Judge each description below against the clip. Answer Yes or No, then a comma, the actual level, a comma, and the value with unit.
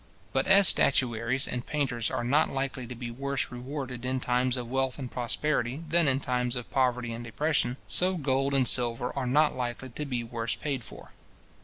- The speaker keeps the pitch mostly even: Yes, narrow, 2.2 semitones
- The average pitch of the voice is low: Yes, low, 130 Hz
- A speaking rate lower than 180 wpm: No, average, 190 wpm